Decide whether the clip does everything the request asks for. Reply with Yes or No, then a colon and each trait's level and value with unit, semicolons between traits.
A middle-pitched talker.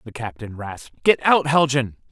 No: low, 130 Hz